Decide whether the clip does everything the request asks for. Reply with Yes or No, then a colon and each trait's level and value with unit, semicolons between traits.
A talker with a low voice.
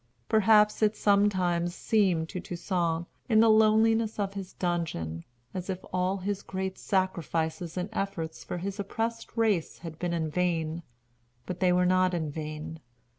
No: medium, 185 Hz